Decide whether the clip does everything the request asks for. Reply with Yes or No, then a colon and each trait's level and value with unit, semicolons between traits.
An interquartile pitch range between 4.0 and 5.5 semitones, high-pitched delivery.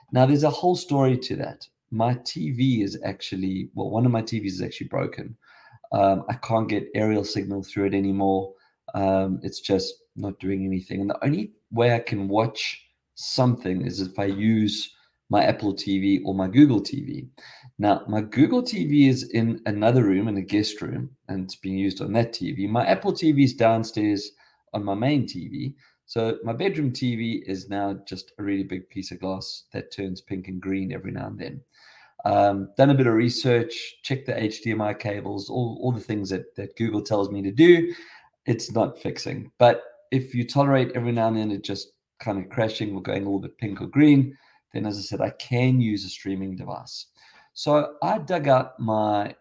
No: average, 4.6 semitones; low, 110 Hz